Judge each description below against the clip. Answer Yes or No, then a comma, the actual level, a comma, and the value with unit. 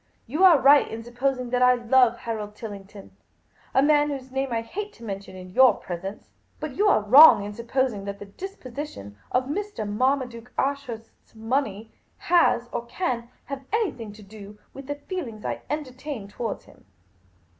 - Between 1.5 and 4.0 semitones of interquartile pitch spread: No, average, 4.7 semitones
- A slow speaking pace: No, average, 170 wpm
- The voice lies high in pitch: Yes, high, 245 Hz